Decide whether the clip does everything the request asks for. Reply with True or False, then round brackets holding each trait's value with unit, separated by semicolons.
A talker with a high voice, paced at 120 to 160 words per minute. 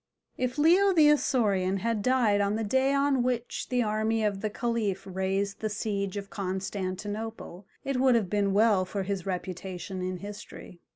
False (205 Hz; 170 wpm)